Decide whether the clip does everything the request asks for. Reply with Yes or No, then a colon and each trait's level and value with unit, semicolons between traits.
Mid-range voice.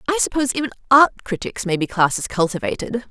No: high, 225 Hz